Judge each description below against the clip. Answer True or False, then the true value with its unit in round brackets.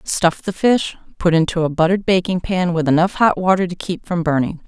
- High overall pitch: False (175 Hz)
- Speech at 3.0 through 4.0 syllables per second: False (5.5 syllables/s)